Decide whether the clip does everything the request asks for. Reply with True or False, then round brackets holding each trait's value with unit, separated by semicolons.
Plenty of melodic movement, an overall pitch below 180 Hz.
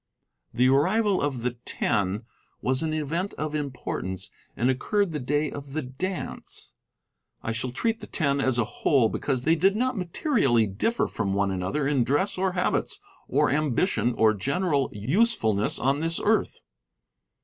True (6.7 semitones; 140 Hz)